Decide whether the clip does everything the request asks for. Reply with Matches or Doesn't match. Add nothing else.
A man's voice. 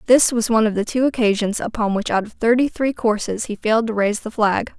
Doesn't match